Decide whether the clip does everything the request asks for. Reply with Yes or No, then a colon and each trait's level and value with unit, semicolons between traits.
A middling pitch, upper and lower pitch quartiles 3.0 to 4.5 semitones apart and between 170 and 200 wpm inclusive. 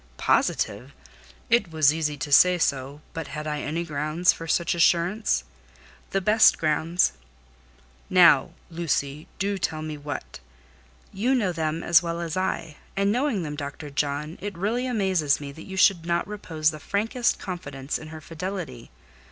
No: medium, 165 Hz; average, 4.1 semitones; average, 160 wpm